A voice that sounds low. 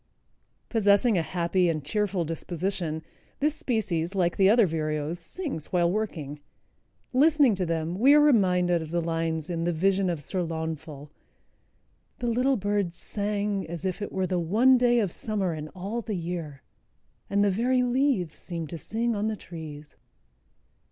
No: medium, 185 Hz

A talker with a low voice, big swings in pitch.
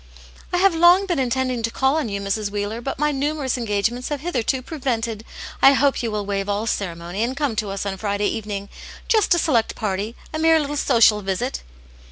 No: high, 230 Hz; wide, 5.7 semitones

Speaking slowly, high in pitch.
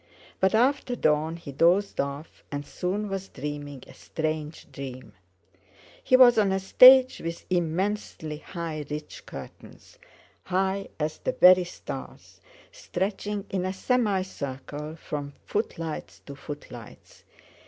No: slow, 120 wpm; medium, 170 Hz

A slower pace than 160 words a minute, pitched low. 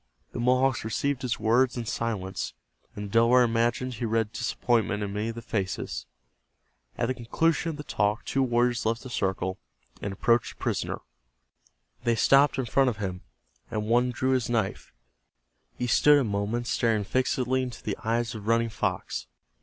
No: average, 175 wpm; low, 115 Hz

